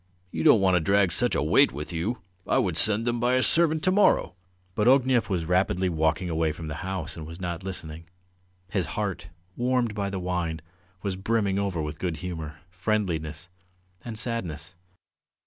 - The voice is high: No, very low, 95 Hz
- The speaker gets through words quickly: No, average, 180 wpm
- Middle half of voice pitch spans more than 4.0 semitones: Yes, average, 4.8 semitones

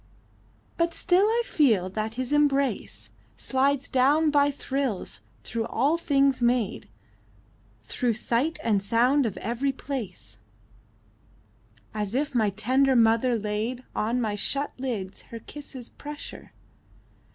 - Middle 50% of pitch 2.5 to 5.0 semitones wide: Yes, average, 4.0 semitones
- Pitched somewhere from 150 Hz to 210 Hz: No, very high, 255 Hz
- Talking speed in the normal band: No, slow, 120 wpm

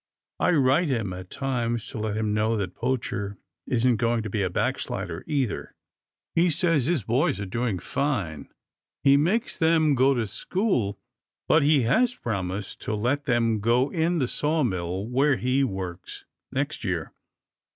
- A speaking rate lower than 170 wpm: Yes, average, 160 wpm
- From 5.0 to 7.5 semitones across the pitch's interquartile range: Yes, wide, 5.6 semitones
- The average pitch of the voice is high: No, low, 120 Hz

